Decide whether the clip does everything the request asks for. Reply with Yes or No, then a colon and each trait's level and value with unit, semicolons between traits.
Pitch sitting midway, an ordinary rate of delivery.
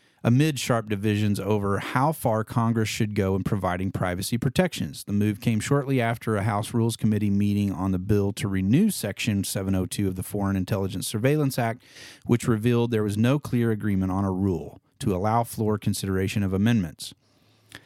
No: low, 105 Hz; average, 175 wpm